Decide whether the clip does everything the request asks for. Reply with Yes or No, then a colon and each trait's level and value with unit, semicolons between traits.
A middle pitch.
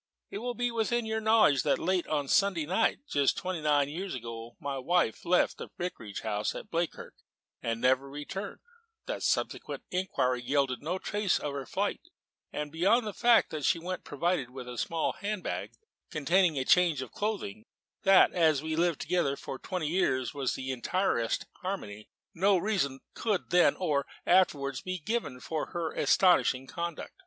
Yes: medium, 165 Hz